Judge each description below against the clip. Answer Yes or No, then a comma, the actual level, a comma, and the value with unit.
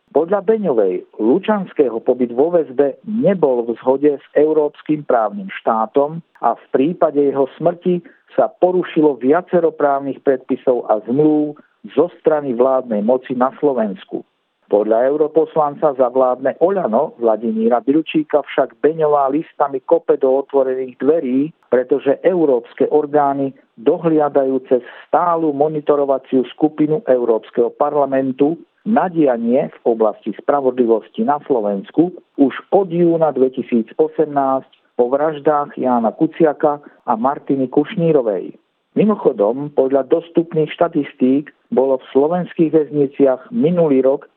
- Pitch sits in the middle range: Yes, medium, 145 Hz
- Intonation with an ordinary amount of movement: Yes, average, 3.7 semitones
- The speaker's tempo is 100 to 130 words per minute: Yes, slow, 110 wpm